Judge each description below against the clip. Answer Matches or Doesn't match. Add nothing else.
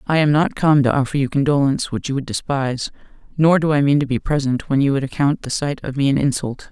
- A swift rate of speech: Matches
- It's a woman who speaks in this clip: Matches